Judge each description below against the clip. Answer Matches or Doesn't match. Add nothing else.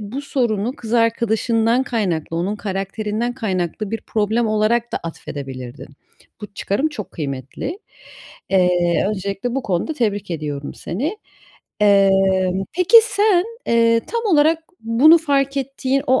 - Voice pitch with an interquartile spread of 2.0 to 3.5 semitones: Doesn't match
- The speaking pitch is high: Matches